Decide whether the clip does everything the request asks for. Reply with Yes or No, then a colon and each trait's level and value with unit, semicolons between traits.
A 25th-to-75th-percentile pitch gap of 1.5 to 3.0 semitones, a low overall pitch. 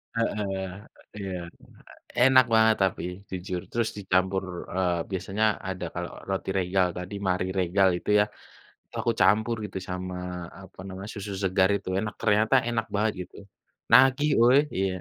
Yes: average, 2.7 semitones; very low, 95 Hz